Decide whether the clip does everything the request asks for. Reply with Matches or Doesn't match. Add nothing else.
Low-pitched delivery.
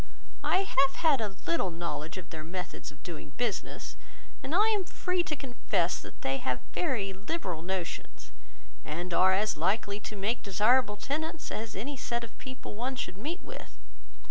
Doesn't match